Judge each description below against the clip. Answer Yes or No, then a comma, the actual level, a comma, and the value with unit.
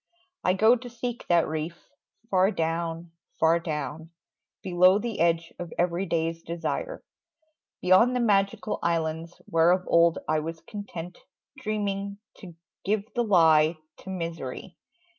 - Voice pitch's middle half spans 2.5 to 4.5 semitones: Yes, average, 3.4 semitones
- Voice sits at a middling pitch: Yes, medium, 175 Hz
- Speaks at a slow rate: Yes, slow, 130 wpm